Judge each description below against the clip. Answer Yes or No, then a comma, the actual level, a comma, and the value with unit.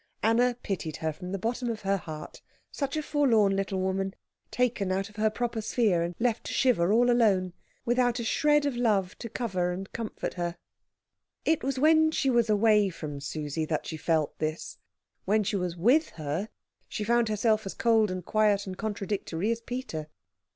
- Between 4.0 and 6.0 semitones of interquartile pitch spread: Yes, average, 4.7 semitones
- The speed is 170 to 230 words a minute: Yes, average, 185 wpm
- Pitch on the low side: No, high, 210 Hz